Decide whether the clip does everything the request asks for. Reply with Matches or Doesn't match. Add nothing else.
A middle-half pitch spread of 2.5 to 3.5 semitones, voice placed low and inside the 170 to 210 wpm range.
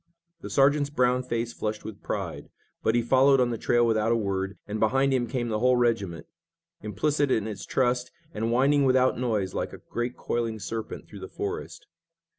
Matches